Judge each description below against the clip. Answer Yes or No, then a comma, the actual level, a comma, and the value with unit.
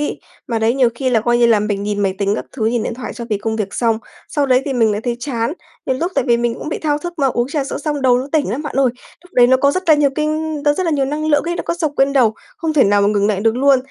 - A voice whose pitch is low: No, very high, 255 Hz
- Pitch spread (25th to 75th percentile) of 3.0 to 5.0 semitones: Yes, average, 4.6 semitones